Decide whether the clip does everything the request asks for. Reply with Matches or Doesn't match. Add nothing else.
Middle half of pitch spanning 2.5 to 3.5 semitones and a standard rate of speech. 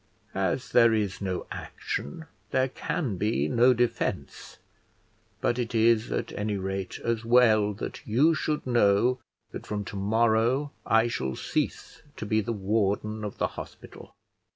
Matches